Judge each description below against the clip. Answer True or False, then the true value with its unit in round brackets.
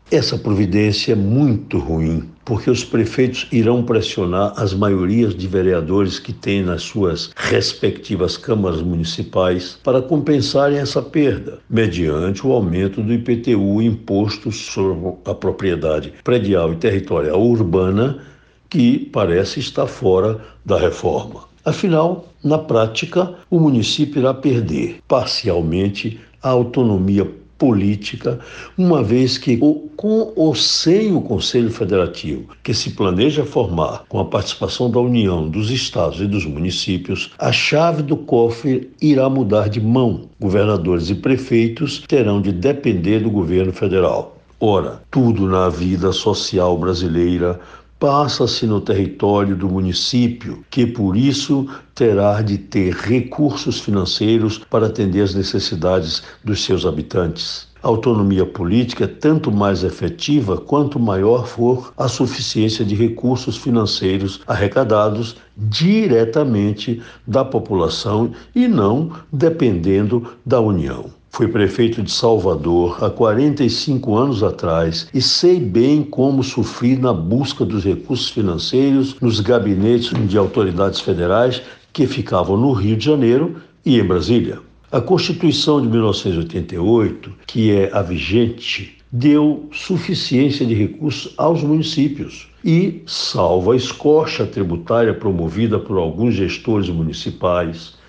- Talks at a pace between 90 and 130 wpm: True (125 wpm)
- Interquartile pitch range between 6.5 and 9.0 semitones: False (5.3 semitones)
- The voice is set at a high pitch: False (115 Hz)